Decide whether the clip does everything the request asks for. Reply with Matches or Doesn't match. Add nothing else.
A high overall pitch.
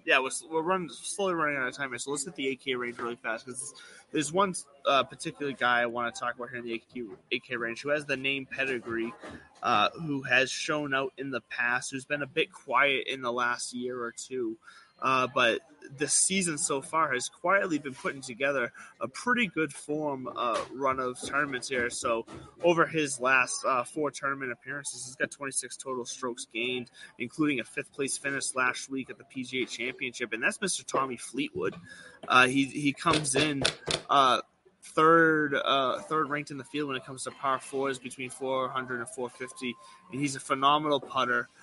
Doesn't match